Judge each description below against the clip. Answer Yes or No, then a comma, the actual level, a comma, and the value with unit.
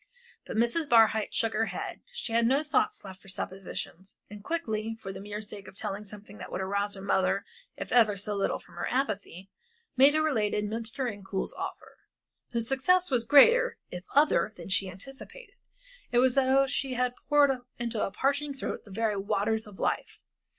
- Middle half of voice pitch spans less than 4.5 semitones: No, average, 5.1 semitones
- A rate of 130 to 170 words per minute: No, average, 185 wpm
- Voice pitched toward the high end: Yes, high, 225 Hz